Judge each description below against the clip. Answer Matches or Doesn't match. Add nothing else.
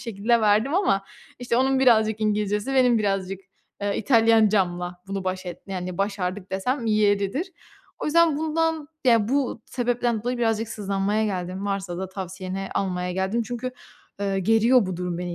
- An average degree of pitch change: Matches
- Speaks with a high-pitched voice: Matches